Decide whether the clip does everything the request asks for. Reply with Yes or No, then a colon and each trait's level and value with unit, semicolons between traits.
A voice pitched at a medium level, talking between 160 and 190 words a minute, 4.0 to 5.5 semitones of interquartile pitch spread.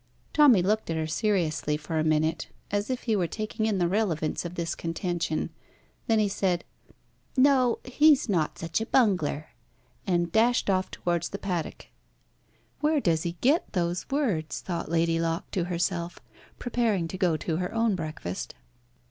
Yes: medium, 180 Hz; average, 165 wpm; average, 4.9 semitones